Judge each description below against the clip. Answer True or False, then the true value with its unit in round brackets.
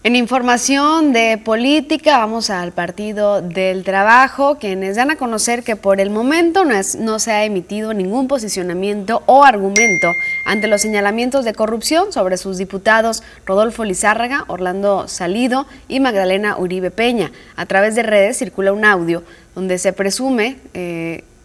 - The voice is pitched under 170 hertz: False (210 Hz)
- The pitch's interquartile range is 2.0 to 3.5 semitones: False (4.3 semitones)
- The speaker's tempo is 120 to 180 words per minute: True (155 wpm)